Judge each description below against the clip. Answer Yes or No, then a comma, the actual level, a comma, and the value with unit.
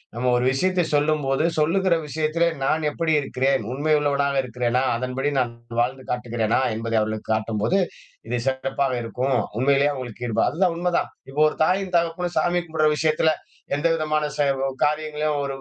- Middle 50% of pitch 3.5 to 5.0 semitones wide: Yes, average, 3.8 semitones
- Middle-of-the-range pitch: Yes, medium, 145 Hz